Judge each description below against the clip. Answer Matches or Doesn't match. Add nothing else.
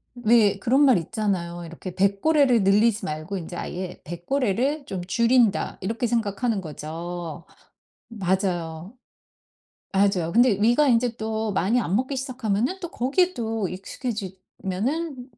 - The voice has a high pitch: Matches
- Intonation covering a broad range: Doesn't match